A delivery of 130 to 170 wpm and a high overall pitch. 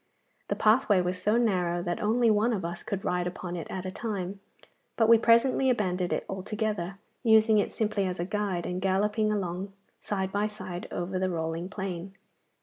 No: average, 185 wpm; high, 195 Hz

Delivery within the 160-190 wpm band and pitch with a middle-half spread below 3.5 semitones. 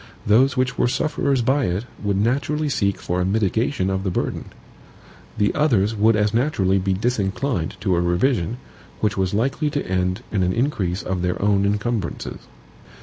No: average, 170 wpm; average, 5.0 semitones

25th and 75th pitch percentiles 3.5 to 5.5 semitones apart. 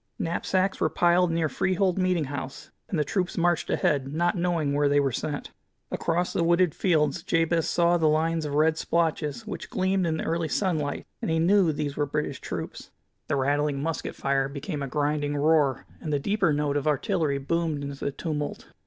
No: average, 3.0 semitones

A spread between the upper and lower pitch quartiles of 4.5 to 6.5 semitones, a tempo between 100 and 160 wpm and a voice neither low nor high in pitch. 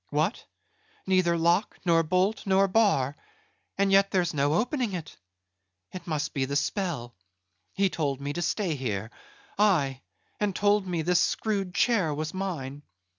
Yes: average, 5.0 semitones; average, 150 wpm; medium, 175 Hz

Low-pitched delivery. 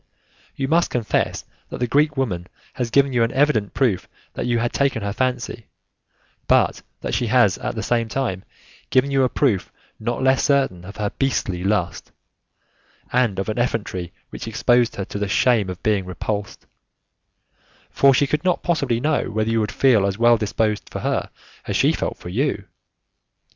Yes: low, 115 Hz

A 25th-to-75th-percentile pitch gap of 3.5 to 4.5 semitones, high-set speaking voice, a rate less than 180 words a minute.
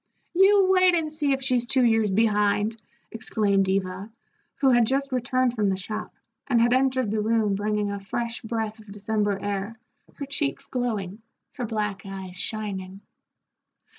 Yes: average, 4.1 semitones; high, 220 Hz; average, 160 wpm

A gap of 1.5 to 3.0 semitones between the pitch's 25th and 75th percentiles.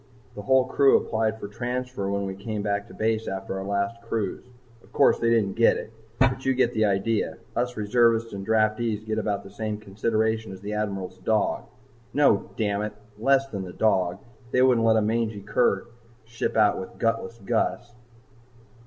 Yes: narrow, 2.4 semitones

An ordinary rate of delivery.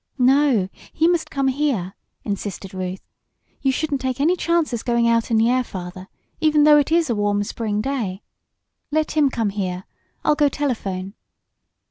Yes: average, 165 wpm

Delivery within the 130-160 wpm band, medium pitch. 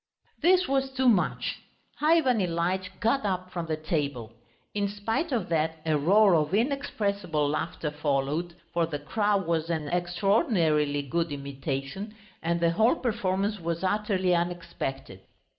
Yes: average, 140 wpm; medium, 175 Hz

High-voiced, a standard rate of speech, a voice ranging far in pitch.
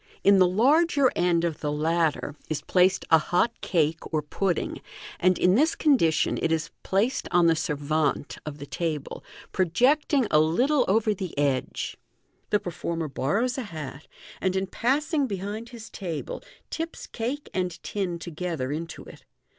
No: medium, 180 Hz; average, 160 wpm; wide, 6.2 semitones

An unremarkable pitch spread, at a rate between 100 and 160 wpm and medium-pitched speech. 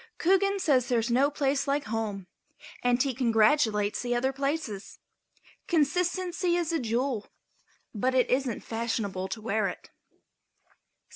No: average, 4.6 semitones; slow, 135 wpm; very high, 255 Hz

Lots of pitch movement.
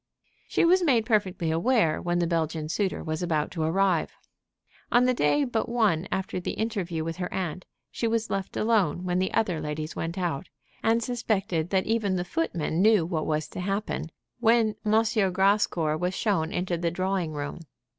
No: average, 4.9 semitones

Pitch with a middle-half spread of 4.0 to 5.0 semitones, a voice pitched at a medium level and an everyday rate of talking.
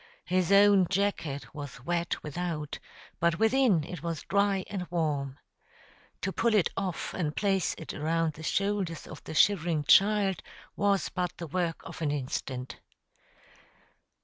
Yes: average, 4.3 semitones; medium, 175 Hz; average, 145 wpm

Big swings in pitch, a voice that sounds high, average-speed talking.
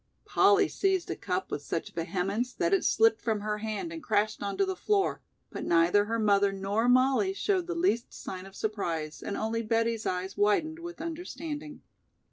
Yes: wide, 8.6 semitones; high, 225 Hz; average, 180 wpm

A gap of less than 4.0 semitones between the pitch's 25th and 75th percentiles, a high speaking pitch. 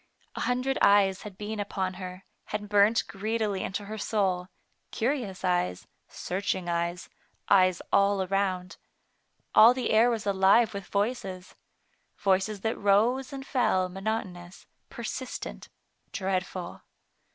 Yes: average, 2.8 semitones; high, 200 Hz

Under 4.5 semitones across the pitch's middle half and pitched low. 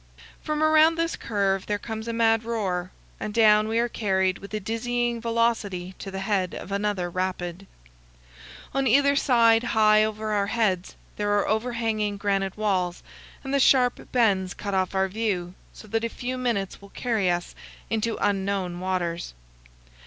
No: average, 3.3 semitones; high, 210 Hz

